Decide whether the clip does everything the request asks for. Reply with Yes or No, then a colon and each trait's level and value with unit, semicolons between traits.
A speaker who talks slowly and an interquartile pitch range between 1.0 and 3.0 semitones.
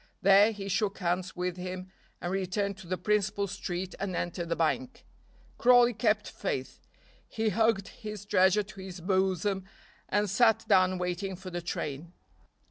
No: average, 155 wpm; narrow, 2.5 semitones